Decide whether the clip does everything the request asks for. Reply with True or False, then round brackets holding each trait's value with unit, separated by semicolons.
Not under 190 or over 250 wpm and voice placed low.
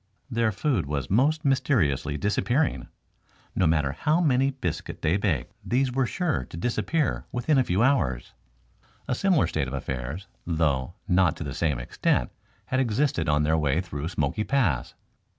False (160 wpm; 95 Hz)